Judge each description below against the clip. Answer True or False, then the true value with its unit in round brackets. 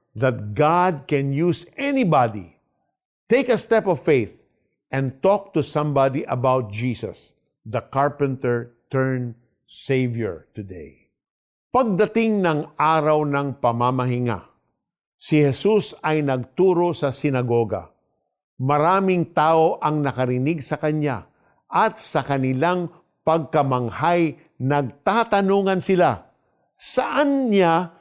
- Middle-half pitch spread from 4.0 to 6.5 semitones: True (5.4 semitones)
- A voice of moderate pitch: True (150 Hz)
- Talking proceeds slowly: True (100 wpm)